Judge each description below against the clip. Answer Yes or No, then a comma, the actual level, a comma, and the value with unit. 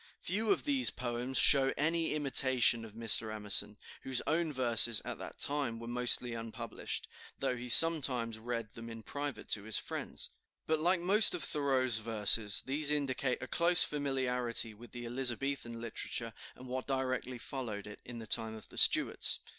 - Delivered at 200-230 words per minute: No, average, 170 wpm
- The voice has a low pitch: Yes, low, 125 Hz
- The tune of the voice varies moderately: Yes, average, 3.7 semitones